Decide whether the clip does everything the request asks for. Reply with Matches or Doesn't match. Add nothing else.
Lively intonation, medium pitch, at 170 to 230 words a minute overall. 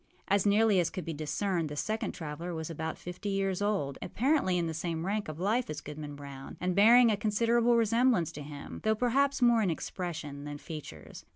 Matches